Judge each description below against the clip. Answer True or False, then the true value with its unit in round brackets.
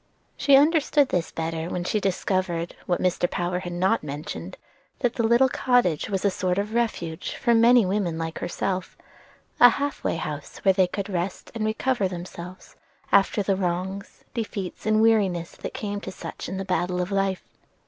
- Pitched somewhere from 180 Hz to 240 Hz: True (190 Hz)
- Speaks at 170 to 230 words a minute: True (180 wpm)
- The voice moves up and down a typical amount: True (3.8 semitones)